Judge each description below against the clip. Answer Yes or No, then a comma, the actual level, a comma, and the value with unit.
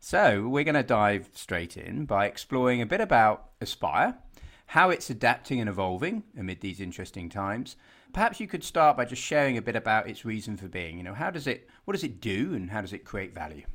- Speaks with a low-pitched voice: Yes, low, 110 Hz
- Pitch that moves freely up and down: Yes, wide, 6.0 semitones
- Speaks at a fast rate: Yes, fast, 225 wpm